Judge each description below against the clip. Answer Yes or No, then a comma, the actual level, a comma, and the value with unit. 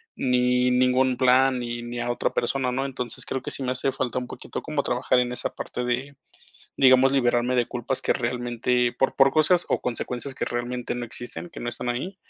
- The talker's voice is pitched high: No, low, 125 Hz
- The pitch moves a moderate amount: No, narrow, 1.5 semitones